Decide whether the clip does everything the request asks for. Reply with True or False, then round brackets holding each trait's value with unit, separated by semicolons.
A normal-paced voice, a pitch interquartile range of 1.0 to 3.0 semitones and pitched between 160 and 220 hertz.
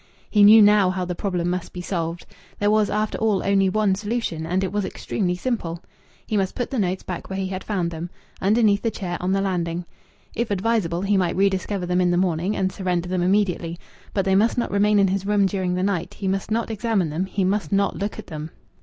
False (235 wpm; 2.5 semitones; 190 Hz)